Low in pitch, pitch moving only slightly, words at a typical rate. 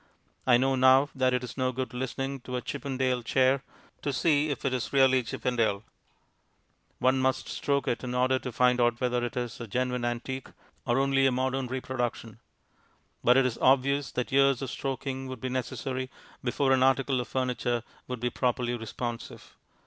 Yes: low, 130 Hz; narrow, 1.4 semitones; average, 180 wpm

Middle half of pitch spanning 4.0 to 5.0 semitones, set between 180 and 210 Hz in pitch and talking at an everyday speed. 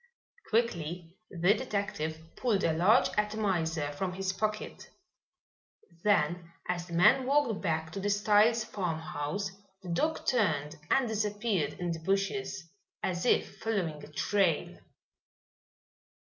No: average, 4.3 semitones; high, 190 Hz; slow, 120 wpm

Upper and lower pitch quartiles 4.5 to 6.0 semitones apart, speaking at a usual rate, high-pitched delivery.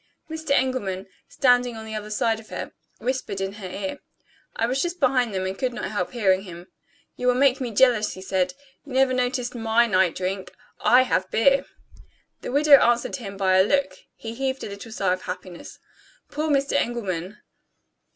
Yes: average, 5.2 semitones; average, 190 wpm; high, 230 Hz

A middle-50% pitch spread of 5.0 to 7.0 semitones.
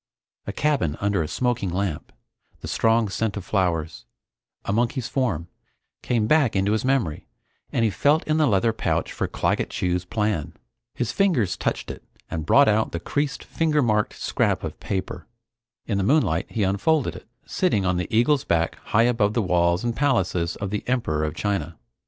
Yes: wide, 5.5 semitones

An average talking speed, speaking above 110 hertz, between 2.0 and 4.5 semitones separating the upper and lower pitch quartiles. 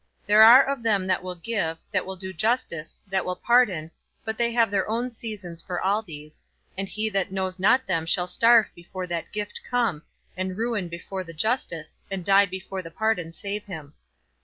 Yes: average, 195 wpm; high, 190 Hz; average, 3.8 semitones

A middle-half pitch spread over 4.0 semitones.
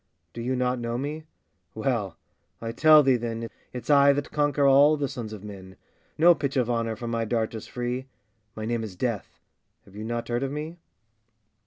No: average, 3.7 semitones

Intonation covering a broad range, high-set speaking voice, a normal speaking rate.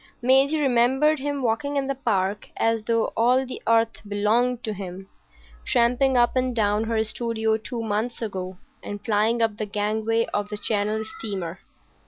No: average, 2.9 semitones; high, 225 Hz; average, 165 wpm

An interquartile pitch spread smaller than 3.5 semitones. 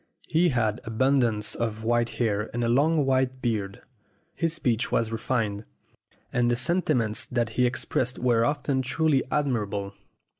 Yes: average, 3.1 semitones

